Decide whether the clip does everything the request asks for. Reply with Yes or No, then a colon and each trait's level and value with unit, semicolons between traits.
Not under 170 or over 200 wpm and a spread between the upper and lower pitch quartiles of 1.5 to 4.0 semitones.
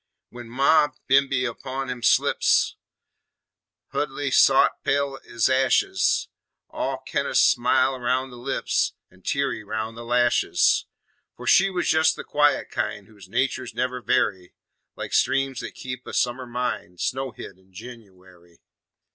No: average, 140 wpm; average, 3.3 semitones